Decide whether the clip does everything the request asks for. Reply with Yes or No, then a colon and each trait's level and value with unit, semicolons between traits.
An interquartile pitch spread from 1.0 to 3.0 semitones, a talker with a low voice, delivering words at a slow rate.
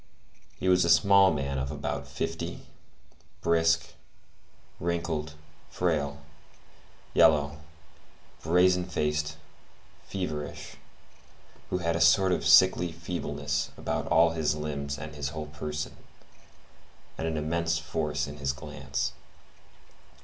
Yes: narrow, 2.5 semitones; very low, 80 Hz; slow, 110 wpm